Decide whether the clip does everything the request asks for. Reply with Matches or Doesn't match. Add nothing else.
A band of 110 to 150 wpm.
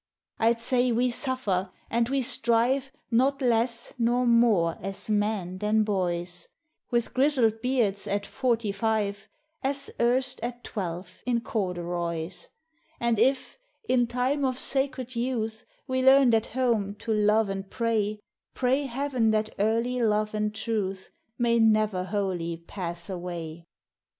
Matches